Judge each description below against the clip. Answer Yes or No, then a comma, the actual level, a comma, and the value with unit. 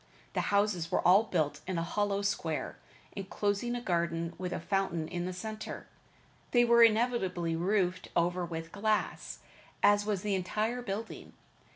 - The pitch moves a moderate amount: Yes, average, 3.7 semitones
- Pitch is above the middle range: Yes, high, 195 Hz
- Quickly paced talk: No, average, 155 wpm